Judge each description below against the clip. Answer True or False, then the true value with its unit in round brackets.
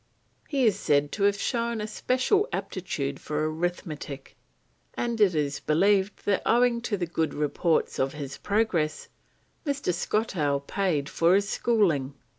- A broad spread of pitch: True (6.5 semitones)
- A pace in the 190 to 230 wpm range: False (145 wpm)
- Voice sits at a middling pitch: True (180 Hz)